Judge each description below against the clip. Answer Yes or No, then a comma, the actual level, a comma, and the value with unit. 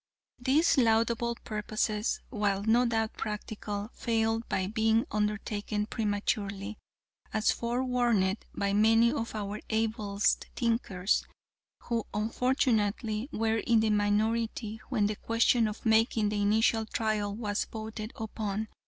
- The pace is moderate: No, slow, 120 wpm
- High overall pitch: Yes, high, 220 Hz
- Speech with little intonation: Yes, narrow, 1.7 semitones